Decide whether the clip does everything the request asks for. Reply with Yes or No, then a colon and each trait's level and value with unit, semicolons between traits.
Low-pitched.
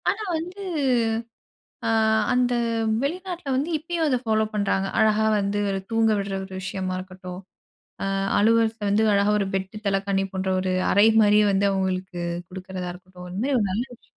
No: high, 200 Hz